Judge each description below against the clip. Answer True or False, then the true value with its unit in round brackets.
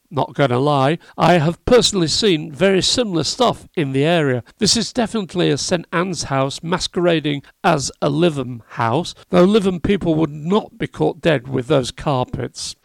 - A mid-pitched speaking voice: True (165 Hz)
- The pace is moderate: True (175 wpm)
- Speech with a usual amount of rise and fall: True (4.3 semitones)